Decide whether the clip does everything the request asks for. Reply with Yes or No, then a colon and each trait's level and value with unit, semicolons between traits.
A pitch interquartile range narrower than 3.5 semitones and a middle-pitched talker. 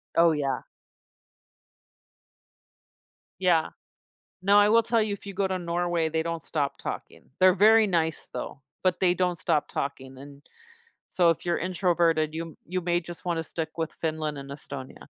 Yes: average, 2.7 semitones; medium, 170 Hz